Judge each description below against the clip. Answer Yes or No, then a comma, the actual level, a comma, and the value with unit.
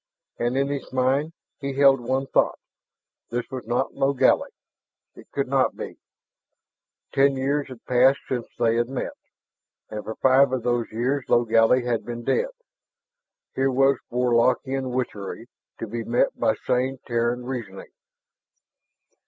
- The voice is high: No, low, 125 Hz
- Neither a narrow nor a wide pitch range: No, narrow, 2.2 semitones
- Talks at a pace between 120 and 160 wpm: Yes, average, 140 wpm